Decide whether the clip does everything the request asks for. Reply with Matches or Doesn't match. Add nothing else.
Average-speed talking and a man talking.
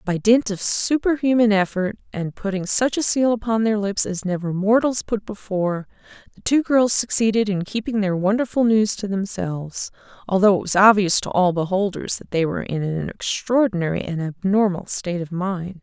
Doesn't match